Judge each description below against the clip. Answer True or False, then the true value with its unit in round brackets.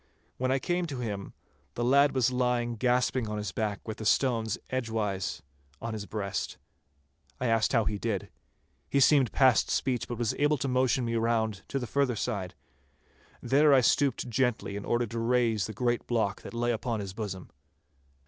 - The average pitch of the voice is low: True (120 Hz)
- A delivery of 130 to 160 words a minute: False (185 wpm)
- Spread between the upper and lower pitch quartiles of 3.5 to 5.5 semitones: False (2.9 semitones)